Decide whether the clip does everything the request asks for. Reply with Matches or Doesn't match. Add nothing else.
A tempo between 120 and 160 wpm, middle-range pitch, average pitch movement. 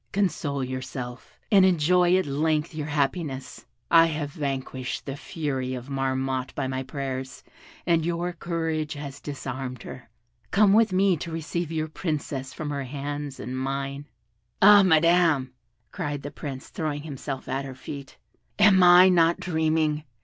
Matches